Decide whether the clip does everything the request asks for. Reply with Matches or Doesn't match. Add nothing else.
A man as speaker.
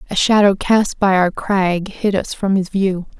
Doesn't match